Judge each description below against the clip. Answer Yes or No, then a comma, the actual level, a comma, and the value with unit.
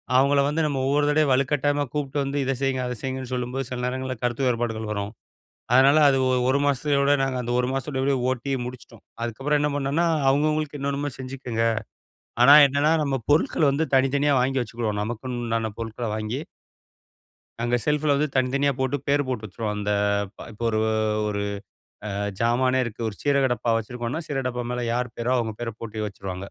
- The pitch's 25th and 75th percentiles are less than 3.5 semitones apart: Yes, average, 3.0 semitones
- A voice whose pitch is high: No, low, 130 Hz